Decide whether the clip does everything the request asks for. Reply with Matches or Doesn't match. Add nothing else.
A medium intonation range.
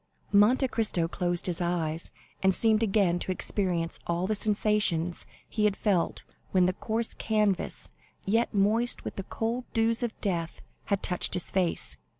Matches